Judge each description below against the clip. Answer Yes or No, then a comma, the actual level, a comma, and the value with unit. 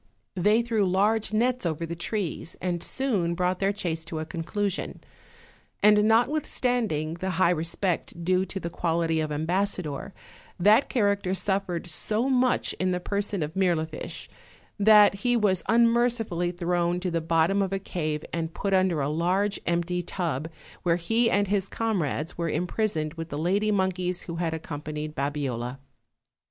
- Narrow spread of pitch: No, average, 3.7 semitones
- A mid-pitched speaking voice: Yes, medium, 180 Hz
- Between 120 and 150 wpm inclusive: No, average, 160 wpm